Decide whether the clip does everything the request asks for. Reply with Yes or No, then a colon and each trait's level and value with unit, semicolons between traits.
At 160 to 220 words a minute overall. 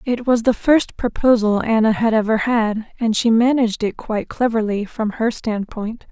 Yes: average, 175 wpm